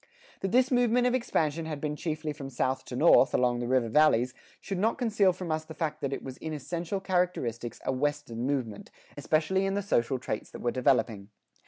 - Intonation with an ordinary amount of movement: No, wide, 6.3 semitones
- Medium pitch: Yes, medium, 150 Hz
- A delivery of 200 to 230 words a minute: Yes, fast, 205 wpm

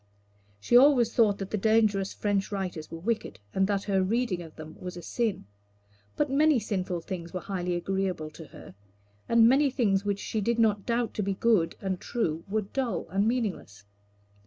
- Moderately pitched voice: No, high, 200 Hz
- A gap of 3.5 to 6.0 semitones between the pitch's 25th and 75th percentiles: Yes, average, 4.1 semitones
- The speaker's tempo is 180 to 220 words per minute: Yes, average, 185 wpm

